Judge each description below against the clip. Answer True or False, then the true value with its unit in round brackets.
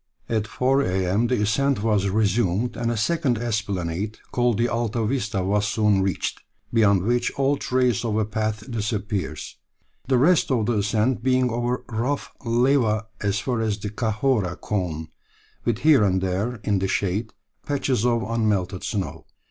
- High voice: False (110 Hz)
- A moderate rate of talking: True (160 wpm)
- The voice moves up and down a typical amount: True (3.3 semitones)